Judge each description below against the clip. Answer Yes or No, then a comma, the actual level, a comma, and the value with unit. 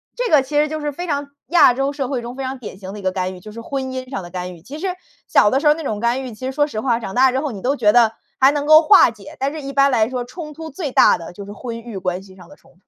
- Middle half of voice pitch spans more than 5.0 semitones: Yes, wide, 5.4 semitones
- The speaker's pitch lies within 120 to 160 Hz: No, very high, 255 Hz